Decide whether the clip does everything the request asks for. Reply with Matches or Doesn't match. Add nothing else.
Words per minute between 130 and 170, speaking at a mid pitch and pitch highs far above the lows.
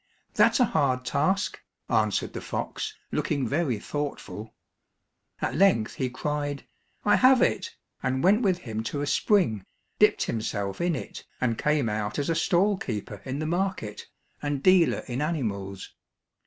Matches